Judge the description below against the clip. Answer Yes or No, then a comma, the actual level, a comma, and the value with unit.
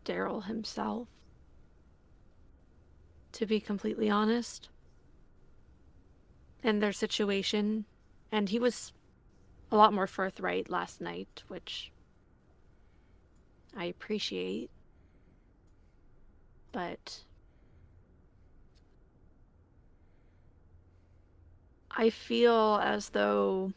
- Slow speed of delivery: Yes, slow, 65 wpm